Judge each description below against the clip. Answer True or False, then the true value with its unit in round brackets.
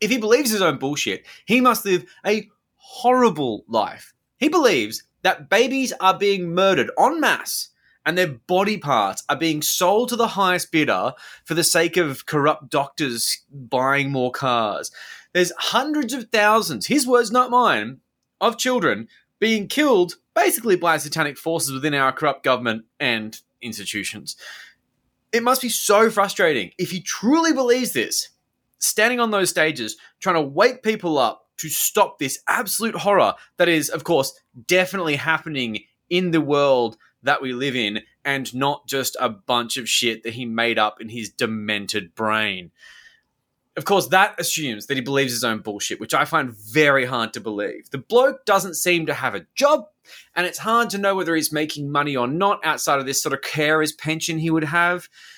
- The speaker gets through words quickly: False (175 wpm)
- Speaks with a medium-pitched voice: True (160 Hz)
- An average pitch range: False (7.6 semitones)